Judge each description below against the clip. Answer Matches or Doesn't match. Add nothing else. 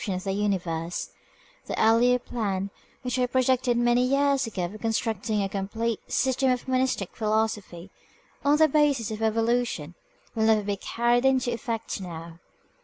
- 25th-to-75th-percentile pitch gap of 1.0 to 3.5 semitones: Doesn't match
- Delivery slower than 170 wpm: Matches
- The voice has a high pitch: Matches